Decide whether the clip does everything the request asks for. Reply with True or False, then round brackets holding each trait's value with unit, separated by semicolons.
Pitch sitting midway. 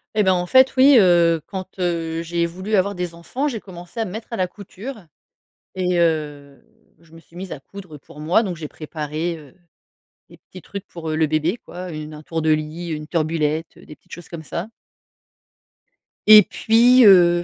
True (175 Hz)